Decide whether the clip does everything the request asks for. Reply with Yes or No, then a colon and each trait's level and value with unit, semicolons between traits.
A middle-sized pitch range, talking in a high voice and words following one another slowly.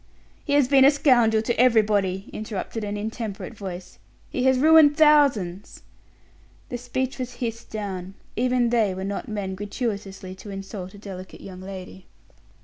No: average, 4.5 semitones; high, 215 Hz; average, 150 wpm